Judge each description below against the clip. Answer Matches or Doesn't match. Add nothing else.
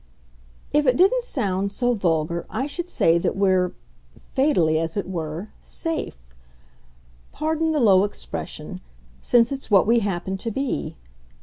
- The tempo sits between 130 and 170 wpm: Matches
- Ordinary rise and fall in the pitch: Doesn't match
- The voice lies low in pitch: Doesn't match